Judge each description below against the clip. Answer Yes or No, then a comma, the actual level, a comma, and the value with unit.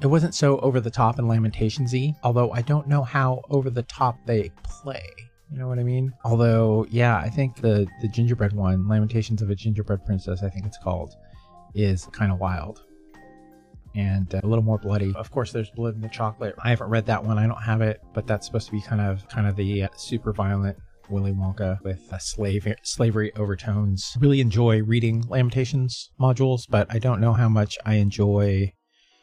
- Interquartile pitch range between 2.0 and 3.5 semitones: Yes, average, 3.1 semitones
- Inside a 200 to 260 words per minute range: Yes, fast, 205 wpm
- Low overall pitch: Yes, low, 110 Hz